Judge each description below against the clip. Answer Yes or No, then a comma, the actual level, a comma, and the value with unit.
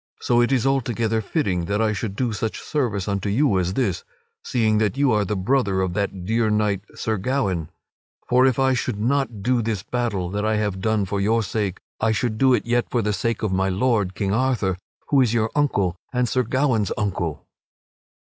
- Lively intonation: No, average, 3.8 semitones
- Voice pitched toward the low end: Yes, low, 110 Hz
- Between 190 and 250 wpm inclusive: Yes, fast, 205 wpm